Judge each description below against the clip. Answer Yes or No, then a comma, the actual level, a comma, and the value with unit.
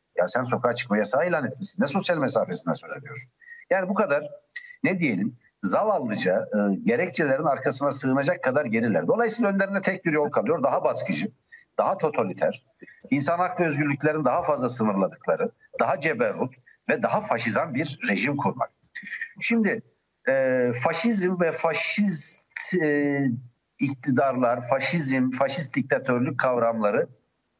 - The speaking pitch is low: No, medium, 160 Hz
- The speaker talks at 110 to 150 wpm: Yes, average, 130 wpm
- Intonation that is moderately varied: No, wide, 7.8 semitones